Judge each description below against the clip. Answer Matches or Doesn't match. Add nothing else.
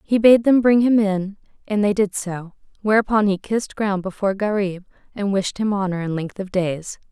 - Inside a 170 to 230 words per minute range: Matches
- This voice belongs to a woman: Matches